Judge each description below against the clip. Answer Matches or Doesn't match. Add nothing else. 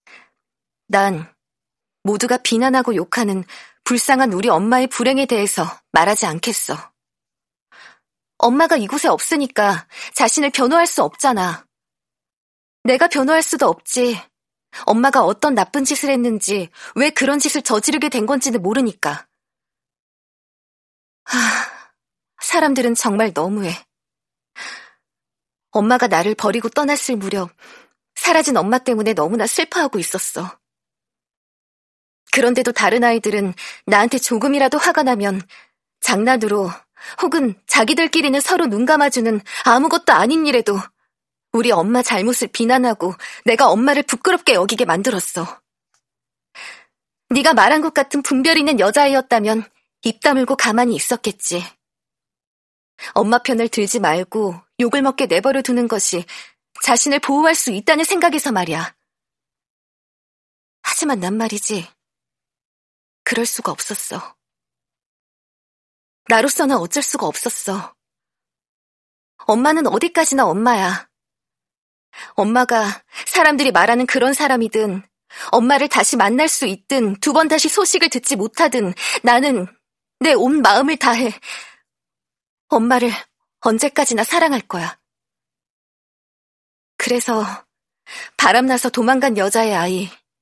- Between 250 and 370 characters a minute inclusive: Matches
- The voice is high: Matches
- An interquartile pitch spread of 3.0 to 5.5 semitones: Matches